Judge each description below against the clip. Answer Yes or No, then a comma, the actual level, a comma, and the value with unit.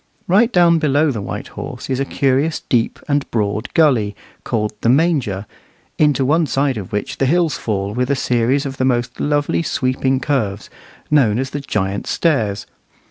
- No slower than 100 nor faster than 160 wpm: No, average, 175 wpm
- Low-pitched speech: Yes, low, 130 Hz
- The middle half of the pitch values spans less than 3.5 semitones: No, average, 4.8 semitones